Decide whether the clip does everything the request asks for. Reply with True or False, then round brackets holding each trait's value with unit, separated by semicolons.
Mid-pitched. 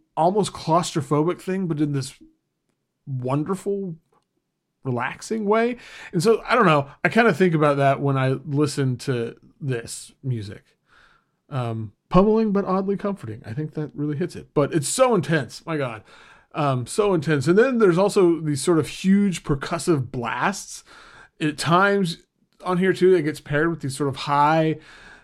True (155 Hz)